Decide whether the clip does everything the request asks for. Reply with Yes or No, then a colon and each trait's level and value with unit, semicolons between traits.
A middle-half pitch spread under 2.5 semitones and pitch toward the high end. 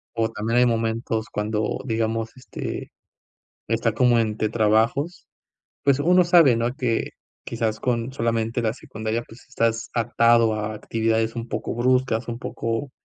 No: narrow, 1.5 semitones; low, 115 Hz